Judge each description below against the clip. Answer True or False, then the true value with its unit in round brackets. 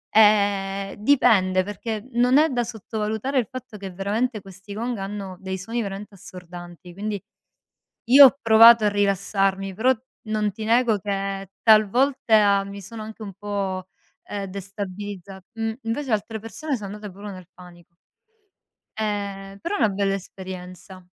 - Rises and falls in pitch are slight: True (2.3 semitones)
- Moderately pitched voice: False (205 Hz)